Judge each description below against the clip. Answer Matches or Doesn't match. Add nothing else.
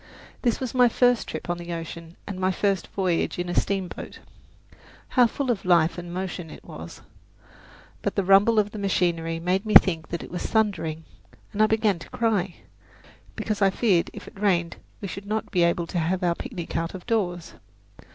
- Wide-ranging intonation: Doesn't match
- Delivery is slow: Doesn't match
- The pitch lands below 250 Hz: Matches